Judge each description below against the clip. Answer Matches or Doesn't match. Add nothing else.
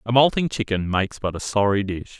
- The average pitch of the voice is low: Matches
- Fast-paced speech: Matches